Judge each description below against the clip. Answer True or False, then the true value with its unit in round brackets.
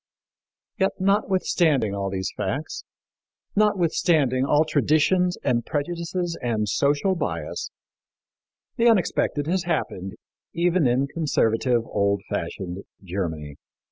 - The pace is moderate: False (100 wpm)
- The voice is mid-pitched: True (145 Hz)